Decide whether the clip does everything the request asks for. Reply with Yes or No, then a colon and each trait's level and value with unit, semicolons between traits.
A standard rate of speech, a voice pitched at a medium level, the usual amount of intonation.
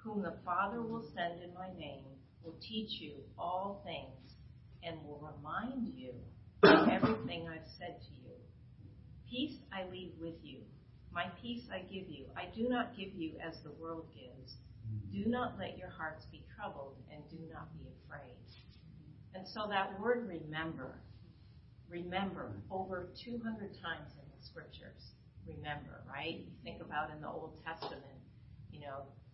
No: average, 160 wpm; medium, 160 Hz; wide, 6.6 semitones